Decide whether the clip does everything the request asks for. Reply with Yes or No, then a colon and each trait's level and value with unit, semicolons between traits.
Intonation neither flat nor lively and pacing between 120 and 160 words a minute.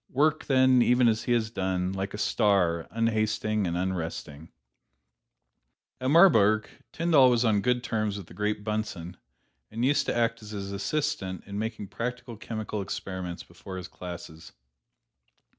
Yes: average, 4.2 semitones; average, 150 wpm